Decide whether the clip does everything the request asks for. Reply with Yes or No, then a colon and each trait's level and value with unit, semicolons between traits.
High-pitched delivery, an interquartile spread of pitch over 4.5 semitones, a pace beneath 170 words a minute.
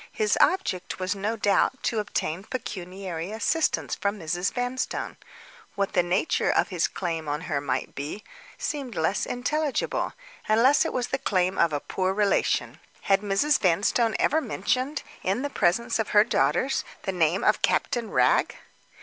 Yes: high, 205 Hz; wide, 5.6 semitones; average, 155 wpm